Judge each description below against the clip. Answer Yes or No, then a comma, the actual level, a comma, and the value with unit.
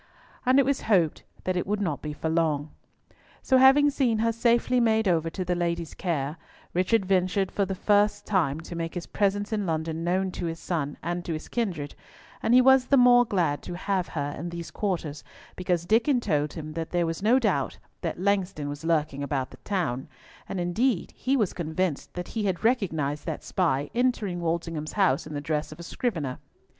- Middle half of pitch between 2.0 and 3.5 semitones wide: No, average, 4.8 semitones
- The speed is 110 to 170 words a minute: No, average, 200 wpm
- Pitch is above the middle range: No, medium, 175 Hz